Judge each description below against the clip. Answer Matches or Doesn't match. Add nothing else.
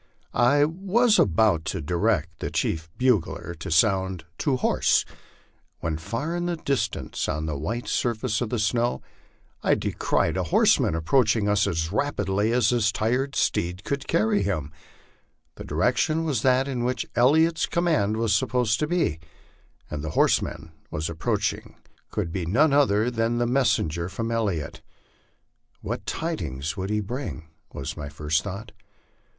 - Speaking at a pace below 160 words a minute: Matches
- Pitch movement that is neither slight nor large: Doesn't match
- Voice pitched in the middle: Doesn't match